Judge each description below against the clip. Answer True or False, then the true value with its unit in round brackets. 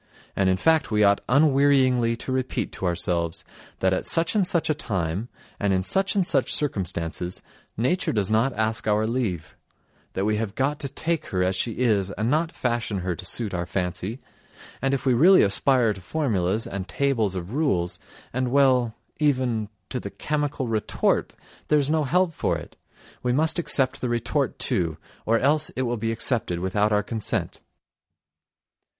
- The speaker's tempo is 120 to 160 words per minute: False (175 wpm)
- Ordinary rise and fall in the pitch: False (6.0 semitones)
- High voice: False (115 Hz)